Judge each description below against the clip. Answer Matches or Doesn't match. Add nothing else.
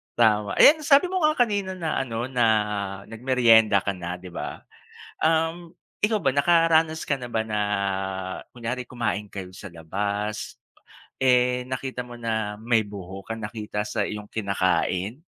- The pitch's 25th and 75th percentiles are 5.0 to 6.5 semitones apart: Matches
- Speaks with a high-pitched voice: Doesn't match